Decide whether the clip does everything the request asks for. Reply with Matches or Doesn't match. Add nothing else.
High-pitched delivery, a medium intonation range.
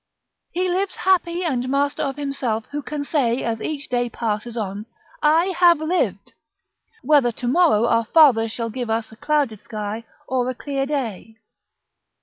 Matches